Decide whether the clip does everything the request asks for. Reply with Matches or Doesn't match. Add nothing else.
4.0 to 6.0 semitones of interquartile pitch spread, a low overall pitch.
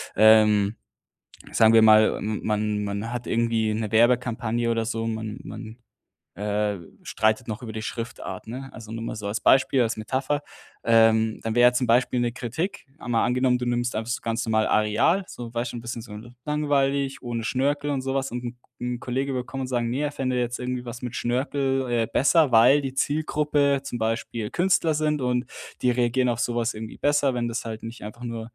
Doesn't match